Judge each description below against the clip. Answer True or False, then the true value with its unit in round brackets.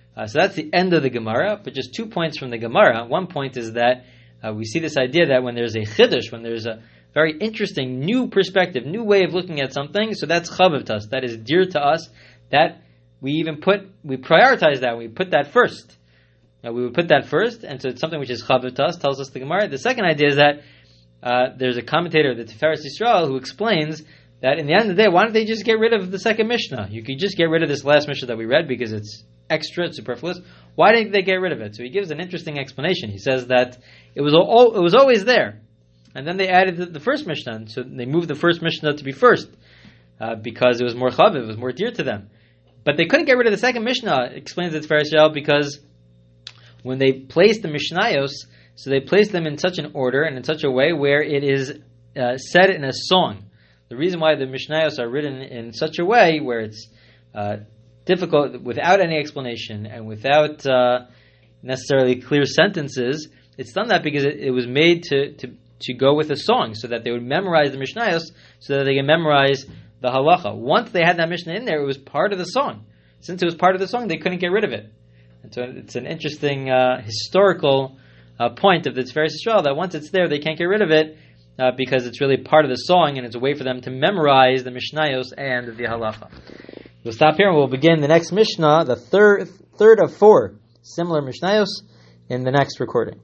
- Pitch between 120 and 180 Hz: True (140 Hz)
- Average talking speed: False (230 wpm)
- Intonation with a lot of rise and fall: True (5.8 semitones)